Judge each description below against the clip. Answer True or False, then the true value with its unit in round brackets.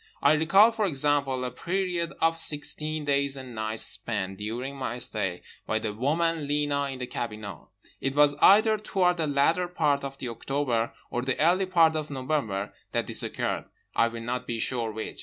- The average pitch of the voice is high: False (140 Hz)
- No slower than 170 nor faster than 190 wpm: True (180 wpm)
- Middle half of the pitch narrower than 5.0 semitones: False (5.3 semitones)